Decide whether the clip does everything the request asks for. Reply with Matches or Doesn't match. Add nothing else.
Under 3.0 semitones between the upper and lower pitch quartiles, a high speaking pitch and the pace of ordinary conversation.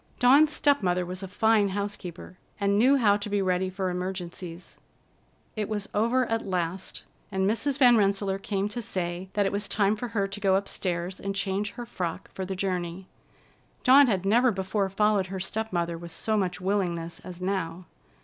Matches